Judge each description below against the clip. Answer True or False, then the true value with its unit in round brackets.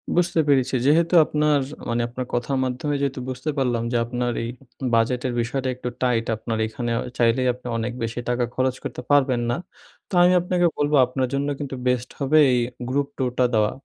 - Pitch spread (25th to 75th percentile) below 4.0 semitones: True (2.6 semitones)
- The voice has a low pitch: True (130 Hz)